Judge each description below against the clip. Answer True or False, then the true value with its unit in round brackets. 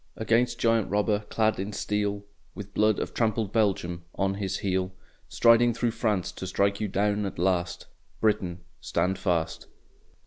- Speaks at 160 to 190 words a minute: False (150 wpm)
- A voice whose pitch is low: True (100 Hz)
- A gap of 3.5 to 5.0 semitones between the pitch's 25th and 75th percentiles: False (2.4 semitones)